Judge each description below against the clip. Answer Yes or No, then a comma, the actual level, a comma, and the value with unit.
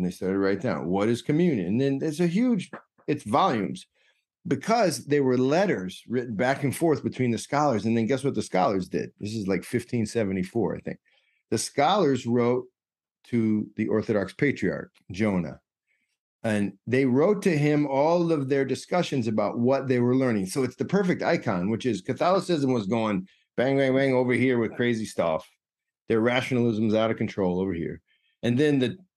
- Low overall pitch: Yes, low, 125 Hz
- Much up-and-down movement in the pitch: No, average, 4.1 semitones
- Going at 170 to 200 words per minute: Yes, average, 185 wpm